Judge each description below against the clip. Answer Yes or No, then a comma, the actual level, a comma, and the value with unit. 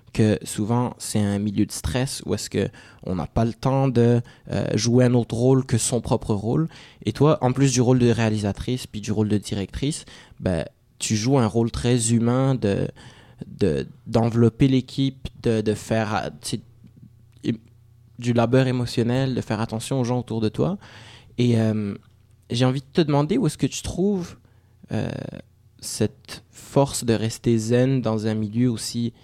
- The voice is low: Yes, low, 120 Hz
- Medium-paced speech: Yes, average, 180 wpm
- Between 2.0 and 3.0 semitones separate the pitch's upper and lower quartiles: Yes, narrow, 2.6 semitones